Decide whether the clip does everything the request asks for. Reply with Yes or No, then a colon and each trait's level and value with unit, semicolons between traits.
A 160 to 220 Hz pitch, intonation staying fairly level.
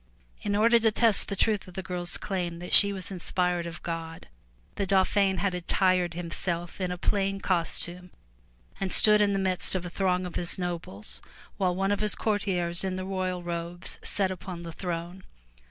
Yes: medium, 185 Hz; narrow, 2.0 semitones